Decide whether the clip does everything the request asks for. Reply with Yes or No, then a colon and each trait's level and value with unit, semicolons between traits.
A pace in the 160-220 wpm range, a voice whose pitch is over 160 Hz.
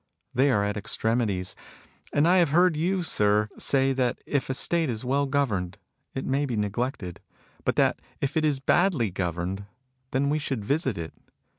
No: average, 175 wpm; low, 130 Hz